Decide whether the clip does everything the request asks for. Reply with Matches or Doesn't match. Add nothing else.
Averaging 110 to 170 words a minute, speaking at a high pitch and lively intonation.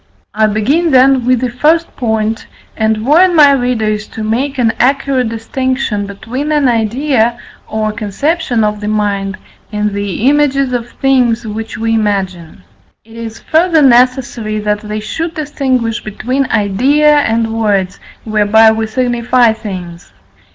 Doesn't match